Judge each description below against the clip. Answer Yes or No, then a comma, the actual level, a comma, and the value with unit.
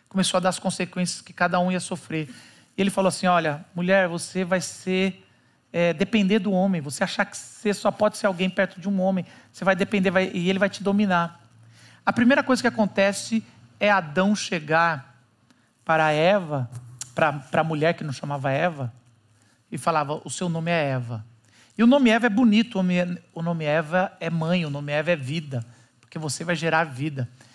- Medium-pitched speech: Yes, medium, 175 Hz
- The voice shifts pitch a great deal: No, average, 5.0 semitones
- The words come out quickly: Yes, fast, 190 wpm